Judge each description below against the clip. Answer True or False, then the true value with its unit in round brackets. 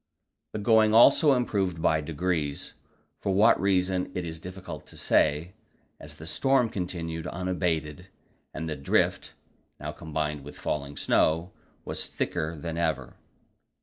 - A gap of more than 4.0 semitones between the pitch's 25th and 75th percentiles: False (3.5 semitones)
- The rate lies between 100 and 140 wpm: True (135 wpm)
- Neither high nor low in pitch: False (85 Hz)